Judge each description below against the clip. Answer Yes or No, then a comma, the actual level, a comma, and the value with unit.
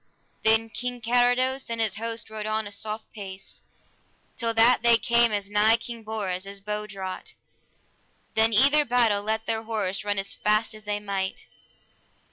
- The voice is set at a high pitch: Yes, high, 220 Hz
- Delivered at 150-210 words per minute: Yes, average, 165 wpm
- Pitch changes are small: Yes, narrow, 2.0 semitones